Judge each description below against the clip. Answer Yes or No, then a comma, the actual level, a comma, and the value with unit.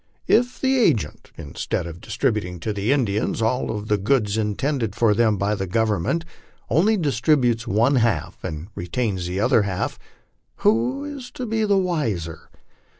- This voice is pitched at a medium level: No, low, 110 Hz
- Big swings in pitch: Yes, wide, 6.5 semitones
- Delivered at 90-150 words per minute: No, average, 160 wpm